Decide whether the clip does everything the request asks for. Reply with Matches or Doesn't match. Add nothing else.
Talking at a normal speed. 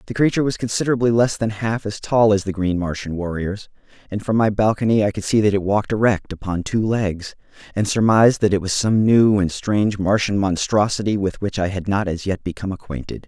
Doesn't match